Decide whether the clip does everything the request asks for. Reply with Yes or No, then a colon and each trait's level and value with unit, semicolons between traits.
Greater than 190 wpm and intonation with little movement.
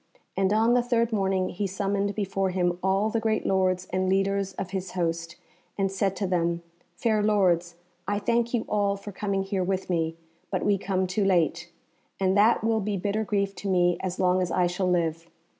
Yes: average, 200 wpm; narrow, 2.1 semitones